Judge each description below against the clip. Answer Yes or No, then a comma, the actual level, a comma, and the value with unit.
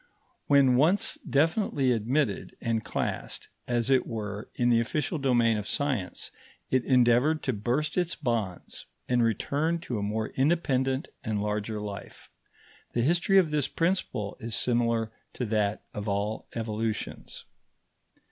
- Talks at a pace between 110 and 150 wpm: Yes, average, 140 wpm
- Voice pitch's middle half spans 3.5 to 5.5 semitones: Yes, average, 4.6 semitones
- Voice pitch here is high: No, low, 120 Hz